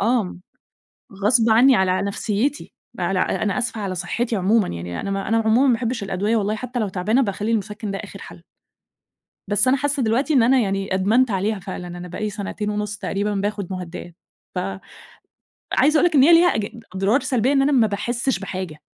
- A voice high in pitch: Yes, high, 210 Hz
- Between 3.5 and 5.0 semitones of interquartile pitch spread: Yes, average, 3.9 semitones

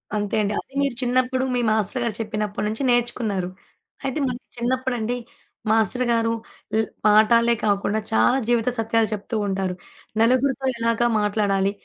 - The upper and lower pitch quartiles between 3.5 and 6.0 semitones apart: No, average, 2.7 semitones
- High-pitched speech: Yes, high, 230 Hz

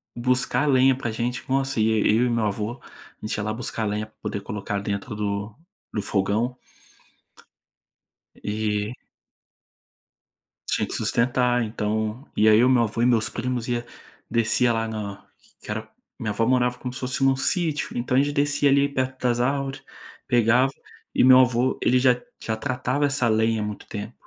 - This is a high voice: No, low, 120 Hz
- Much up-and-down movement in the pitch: No, average, 3.0 semitones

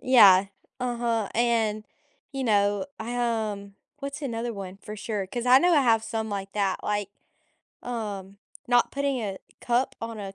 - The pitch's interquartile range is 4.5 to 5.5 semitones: No, average, 3.2 semitones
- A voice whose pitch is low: No, high, 225 Hz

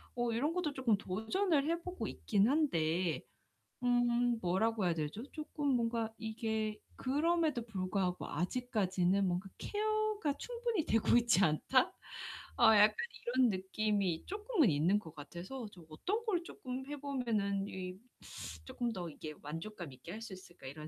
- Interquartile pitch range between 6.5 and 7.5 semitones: Yes, wide, 7.0 semitones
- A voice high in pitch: Yes, high, 220 Hz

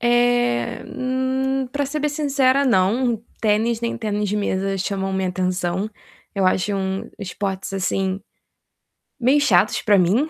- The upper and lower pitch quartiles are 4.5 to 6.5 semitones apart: Yes, average, 5.2 semitones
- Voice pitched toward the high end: Yes, high, 210 Hz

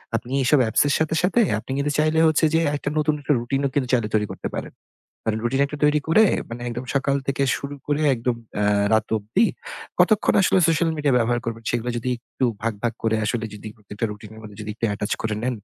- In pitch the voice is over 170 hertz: No, low, 125 Hz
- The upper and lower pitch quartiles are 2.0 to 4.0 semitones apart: No, average, 4.8 semitones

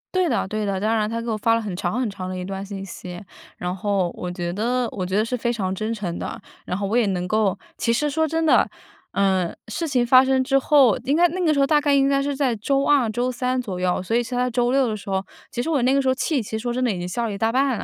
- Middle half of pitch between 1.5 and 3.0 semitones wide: No, average, 5.1 semitones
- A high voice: Yes, high, 230 Hz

